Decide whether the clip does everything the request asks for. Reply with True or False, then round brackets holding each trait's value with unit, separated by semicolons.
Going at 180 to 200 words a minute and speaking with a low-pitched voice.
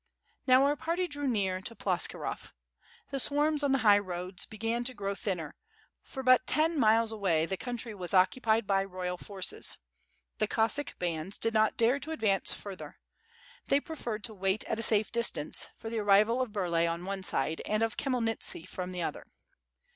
False (185 wpm; 215 Hz)